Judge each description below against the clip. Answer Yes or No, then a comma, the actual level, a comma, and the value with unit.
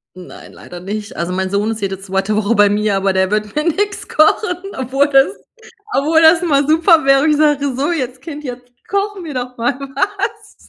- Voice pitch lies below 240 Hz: No, very high, 270 Hz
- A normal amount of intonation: No, wide, 7.1 semitones